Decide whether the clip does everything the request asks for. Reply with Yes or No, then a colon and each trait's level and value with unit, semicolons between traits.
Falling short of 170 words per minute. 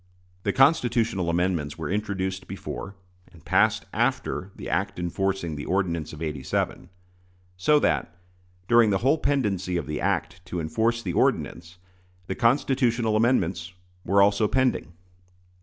Yes: slow, 135 wpm